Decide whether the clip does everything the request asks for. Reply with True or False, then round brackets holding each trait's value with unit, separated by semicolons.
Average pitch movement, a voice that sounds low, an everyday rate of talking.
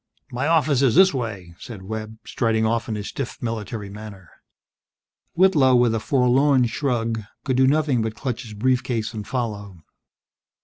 True (3.2 semitones; 115 Hz; 165 wpm)